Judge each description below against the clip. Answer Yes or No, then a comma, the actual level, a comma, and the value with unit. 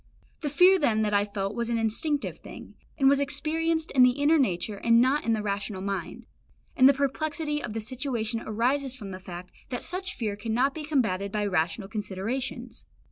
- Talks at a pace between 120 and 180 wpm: No, average, 190 wpm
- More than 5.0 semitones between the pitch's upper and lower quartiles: Yes, wide, 5.4 semitones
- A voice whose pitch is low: No, high, 235 Hz